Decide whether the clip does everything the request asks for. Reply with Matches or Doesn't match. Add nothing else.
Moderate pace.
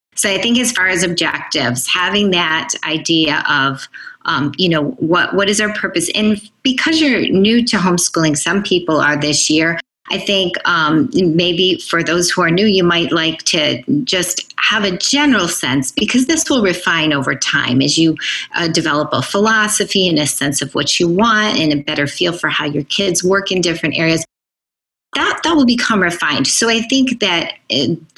Matches